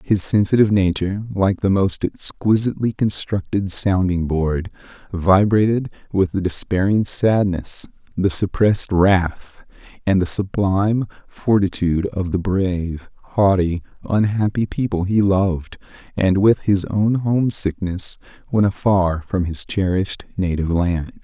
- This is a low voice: Yes, very low, 95 Hz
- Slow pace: Yes, slow, 120 wpm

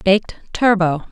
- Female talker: Yes, female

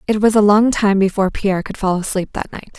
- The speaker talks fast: Yes, fast, 260 wpm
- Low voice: No, high, 200 Hz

